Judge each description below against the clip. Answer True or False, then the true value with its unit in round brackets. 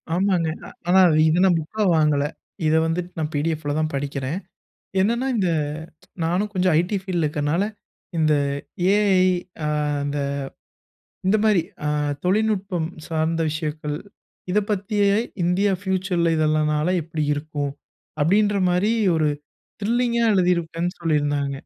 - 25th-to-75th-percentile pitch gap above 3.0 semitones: True (4.1 semitones)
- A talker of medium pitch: True (170 Hz)